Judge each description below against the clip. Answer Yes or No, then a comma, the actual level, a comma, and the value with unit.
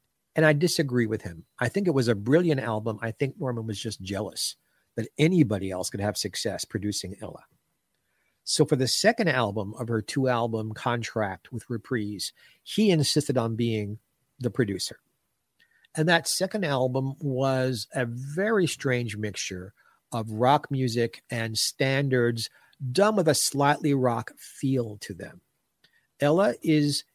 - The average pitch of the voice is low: Yes, low, 125 Hz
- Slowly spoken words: No, average, 150 wpm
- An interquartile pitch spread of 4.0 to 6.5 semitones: Yes, average, 4.7 semitones